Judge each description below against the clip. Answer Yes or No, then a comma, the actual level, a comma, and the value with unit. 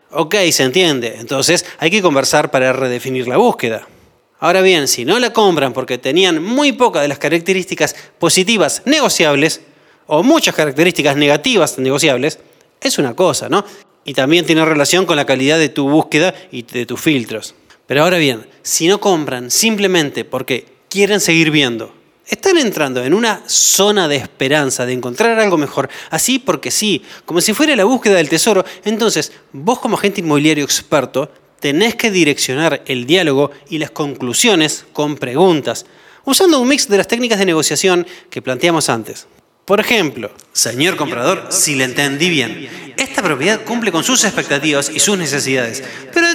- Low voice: No, medium, 160 Hz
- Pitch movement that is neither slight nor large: No, wide, 6.3 semitones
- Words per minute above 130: Yes, average, 165 wpm